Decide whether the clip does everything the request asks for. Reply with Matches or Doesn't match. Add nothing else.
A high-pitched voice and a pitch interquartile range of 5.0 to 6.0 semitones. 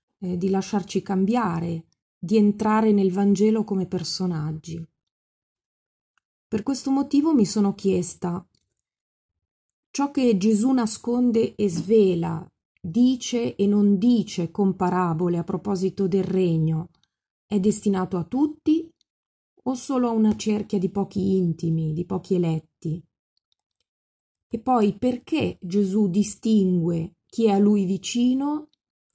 Doesn't match